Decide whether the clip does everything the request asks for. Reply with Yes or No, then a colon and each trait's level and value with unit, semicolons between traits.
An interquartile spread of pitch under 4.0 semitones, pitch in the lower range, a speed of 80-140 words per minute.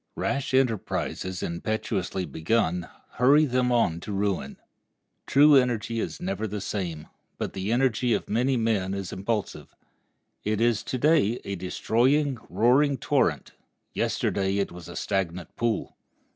No: average, 4.7 semitones; low, 110 Hz; slow, 135 wpm